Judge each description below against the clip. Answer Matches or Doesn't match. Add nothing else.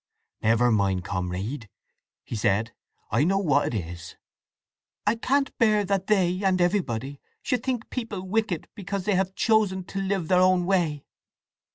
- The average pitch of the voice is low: Doesn't match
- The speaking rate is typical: Matches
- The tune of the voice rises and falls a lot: Matches